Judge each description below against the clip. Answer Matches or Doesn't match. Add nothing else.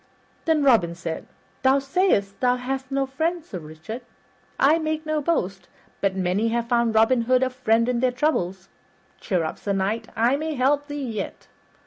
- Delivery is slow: Doesn't match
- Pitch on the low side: Doesn't match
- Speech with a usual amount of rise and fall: Doesn't match